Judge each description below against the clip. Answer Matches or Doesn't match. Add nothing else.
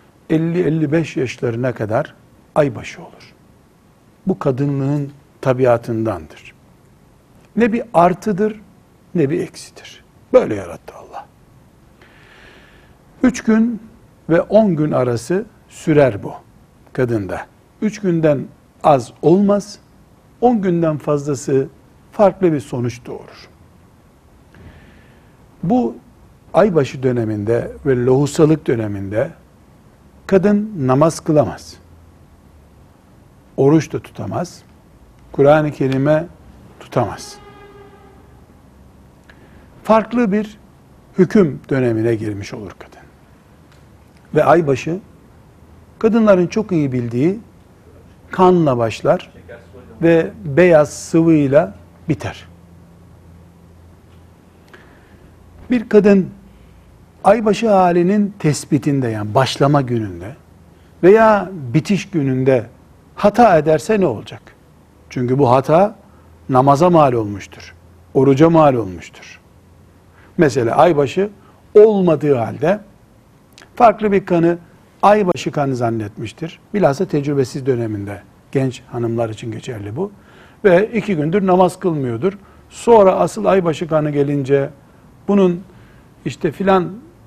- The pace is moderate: Doesn't match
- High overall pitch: Doesn't match